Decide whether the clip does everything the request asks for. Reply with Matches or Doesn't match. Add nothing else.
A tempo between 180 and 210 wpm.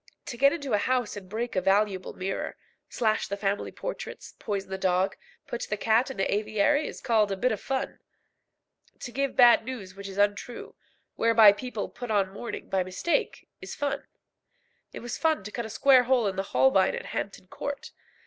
Matches